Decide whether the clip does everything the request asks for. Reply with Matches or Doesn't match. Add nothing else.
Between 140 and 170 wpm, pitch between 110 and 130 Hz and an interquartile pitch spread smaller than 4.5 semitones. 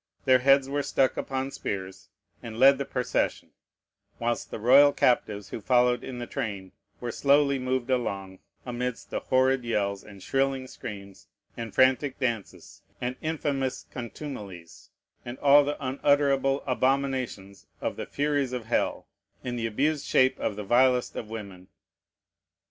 Matches